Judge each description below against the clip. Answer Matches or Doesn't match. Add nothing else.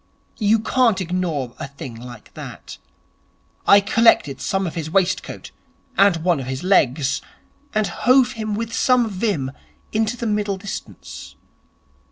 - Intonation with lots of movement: Matches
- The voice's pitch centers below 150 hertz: Doesn't match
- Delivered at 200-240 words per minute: Doesn't match